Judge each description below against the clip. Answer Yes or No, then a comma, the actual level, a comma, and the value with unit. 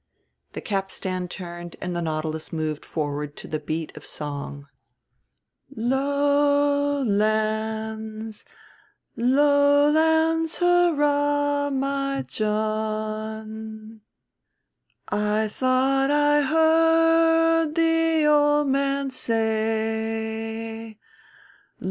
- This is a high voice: Yes, high, 230 Hz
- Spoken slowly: Yes, slow, 75 wpm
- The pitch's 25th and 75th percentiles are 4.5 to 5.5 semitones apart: Yes, average, 5.1 semitones